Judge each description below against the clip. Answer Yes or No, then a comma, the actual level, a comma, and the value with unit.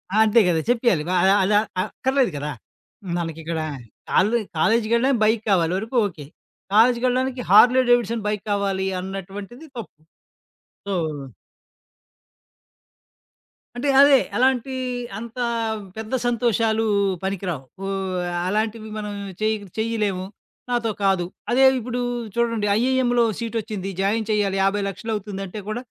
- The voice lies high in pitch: Yes, high, 220 Hz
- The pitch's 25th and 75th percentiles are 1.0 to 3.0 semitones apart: No, average, 3.5 semitones